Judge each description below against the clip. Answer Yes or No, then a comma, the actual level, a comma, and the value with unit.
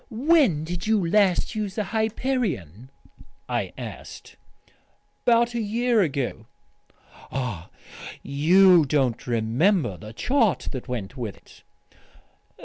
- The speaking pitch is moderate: Yes, medium, 175 Hz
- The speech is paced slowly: Yes, slow, 110 wpm